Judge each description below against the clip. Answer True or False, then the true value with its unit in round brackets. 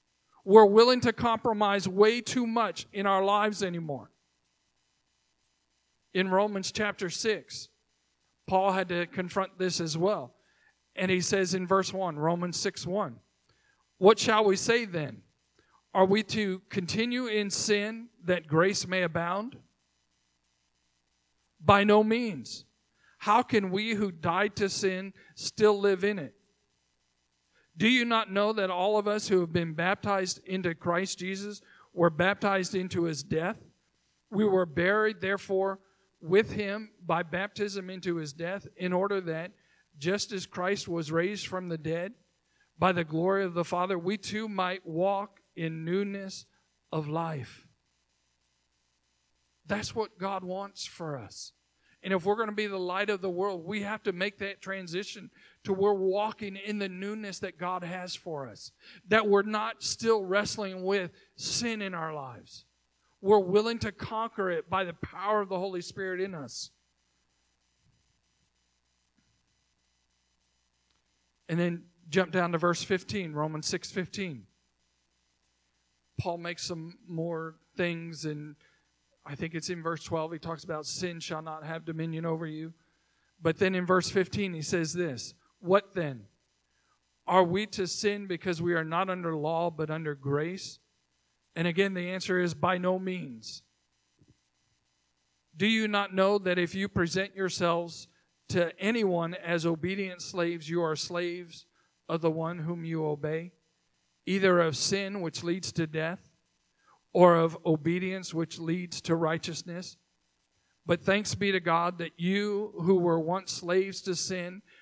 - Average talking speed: True (150 wpm)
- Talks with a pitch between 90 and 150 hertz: False (180 Hz)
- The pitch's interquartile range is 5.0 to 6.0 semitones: False (3.8 semitones)